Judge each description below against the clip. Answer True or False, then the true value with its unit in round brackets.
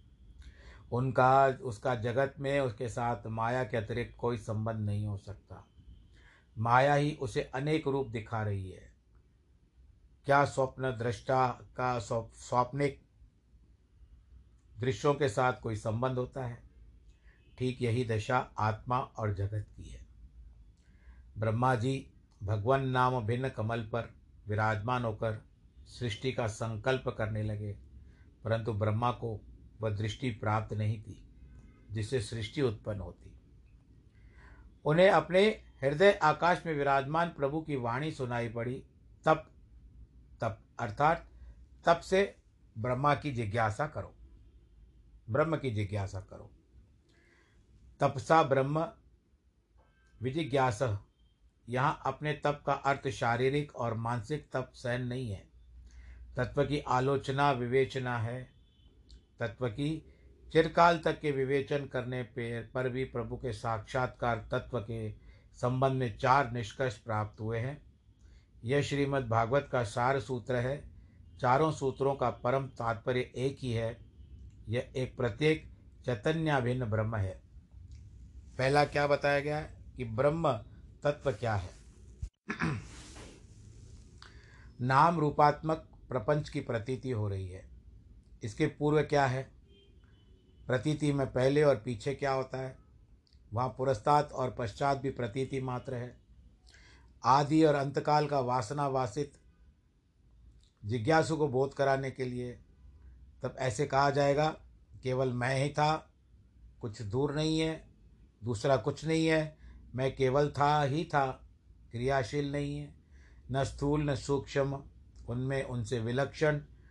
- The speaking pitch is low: True (125 Hz)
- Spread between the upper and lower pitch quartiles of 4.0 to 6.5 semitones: True (4.9 semitones)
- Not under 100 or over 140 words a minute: True (120 wpm)